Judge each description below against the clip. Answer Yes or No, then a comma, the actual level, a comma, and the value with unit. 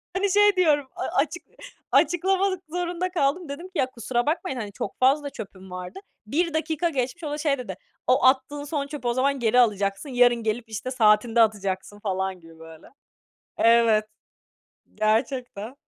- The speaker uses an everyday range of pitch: No, wide, 6.1 semitones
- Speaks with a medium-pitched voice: No, very high, 255 Hz